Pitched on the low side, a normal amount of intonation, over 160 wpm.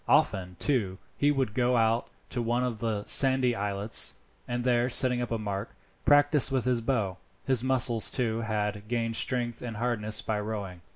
Yes: low, 115 Hz; average, 3.0 semitones; average, 175 wpm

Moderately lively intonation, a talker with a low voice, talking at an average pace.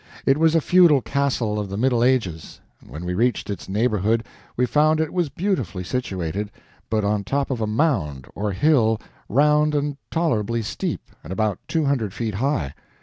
No: wide, 6.1 semitones; low, 115 Hz; average, 175 wpm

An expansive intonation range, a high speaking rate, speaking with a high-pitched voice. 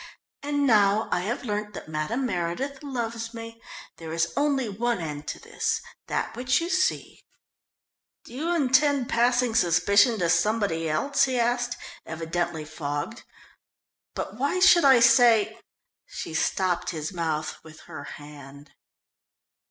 No: wide, 7.1 semitones; average, 145 wpm; high, 225 Hz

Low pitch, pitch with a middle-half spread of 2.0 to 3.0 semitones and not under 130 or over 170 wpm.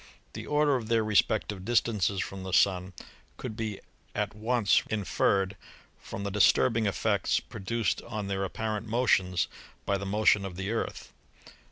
Yes: low, 105 Hz; narrow, 2.6 semitones; average, 150 wpm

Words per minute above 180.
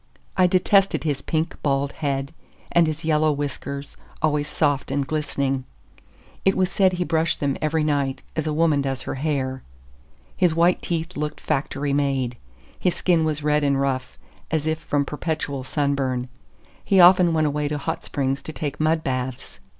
No: average, 170 wpm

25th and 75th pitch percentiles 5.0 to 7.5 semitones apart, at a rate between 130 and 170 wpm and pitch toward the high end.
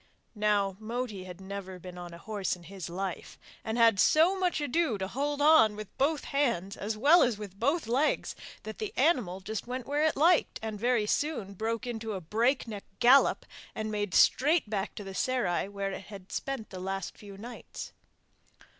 No: average, 5.3 semitones; average, 190 wpm; high, 220 Hz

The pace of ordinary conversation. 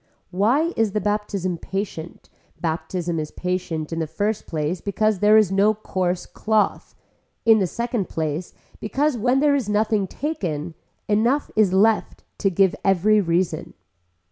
Yes: average, 145 wpm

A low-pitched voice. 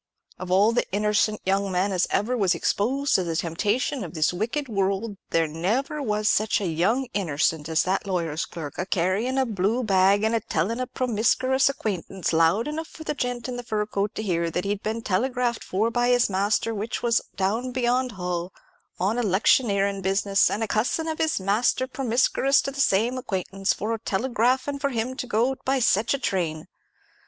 No: high, 210 Hz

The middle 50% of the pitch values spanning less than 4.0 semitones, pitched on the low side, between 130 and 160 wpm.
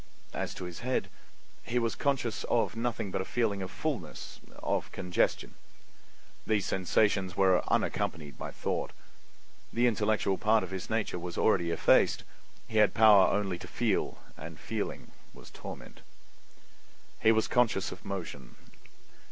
Yes: average, 3.4 semitones; low, 105 Hz; average, 140 wpm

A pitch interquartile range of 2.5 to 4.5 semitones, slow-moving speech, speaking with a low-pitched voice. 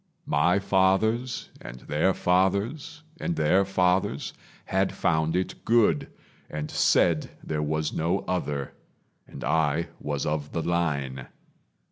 Yes: average, 4.2 semitones; slow, 120 wpm; very low, 85 Hz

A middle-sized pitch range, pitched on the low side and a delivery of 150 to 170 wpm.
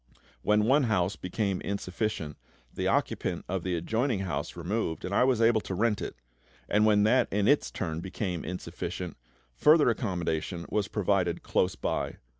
Yes: average, 3.6 semitones; low, 100 Hz; average, 160 wpm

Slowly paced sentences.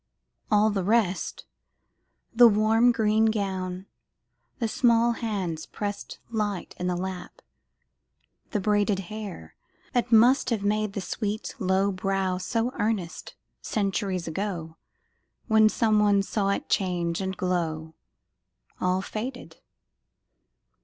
Yes: slow, 115 wpm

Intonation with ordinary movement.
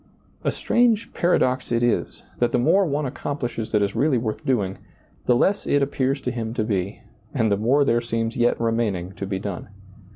Yes: average, 4.3 semitones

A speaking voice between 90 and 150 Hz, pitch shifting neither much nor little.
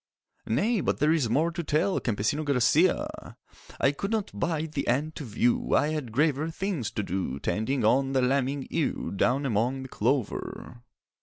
Yes: medium, 140 Hz; average, 4.6 semitones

